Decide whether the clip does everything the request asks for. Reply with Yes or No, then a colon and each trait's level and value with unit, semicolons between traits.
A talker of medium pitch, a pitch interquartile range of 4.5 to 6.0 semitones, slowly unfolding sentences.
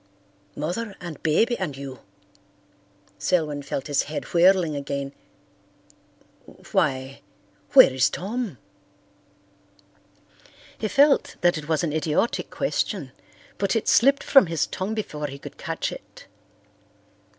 Yes: medium, 160 Hz; wide, 5.6 semitones; slow, 115 wpm